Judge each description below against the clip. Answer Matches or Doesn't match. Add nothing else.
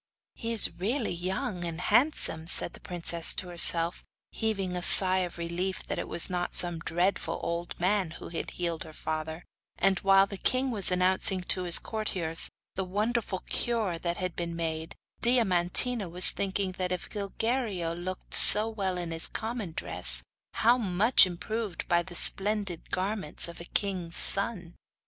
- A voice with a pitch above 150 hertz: Matches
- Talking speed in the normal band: Matches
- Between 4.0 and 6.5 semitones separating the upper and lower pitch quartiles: Doesn't match